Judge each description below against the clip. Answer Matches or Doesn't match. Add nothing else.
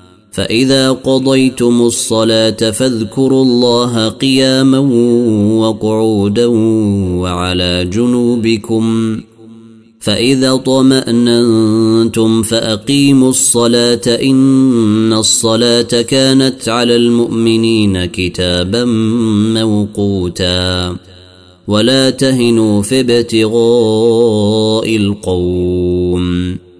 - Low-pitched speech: Matches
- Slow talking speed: Matches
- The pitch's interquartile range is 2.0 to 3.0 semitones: Matches